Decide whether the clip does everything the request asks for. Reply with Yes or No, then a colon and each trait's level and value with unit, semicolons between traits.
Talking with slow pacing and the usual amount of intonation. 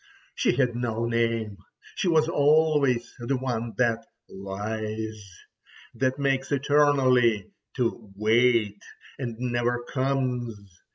Yes: slow, 105 wpm; average, 3.1 semitones